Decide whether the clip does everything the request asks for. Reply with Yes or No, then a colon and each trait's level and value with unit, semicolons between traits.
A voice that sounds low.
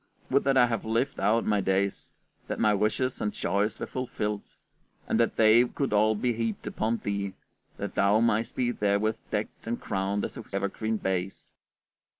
Yes: low, 110 Hz